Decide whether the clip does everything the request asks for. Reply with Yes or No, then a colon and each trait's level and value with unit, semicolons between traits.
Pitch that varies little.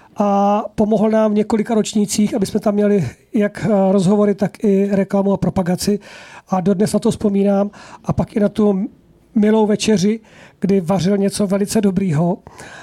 Yes: narrow, 1.4 semitones